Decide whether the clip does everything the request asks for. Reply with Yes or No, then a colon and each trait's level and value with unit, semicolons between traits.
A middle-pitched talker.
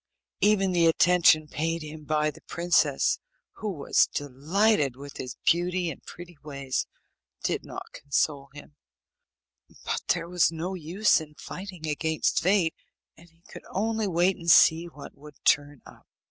Yes: medium, 165 Hz